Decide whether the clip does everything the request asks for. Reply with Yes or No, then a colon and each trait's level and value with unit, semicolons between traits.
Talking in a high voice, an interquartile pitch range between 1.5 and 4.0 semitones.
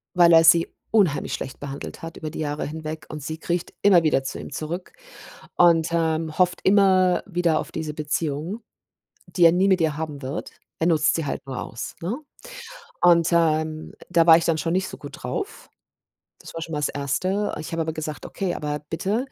No: medium, 165 Hz; narrow, 2.4 semitones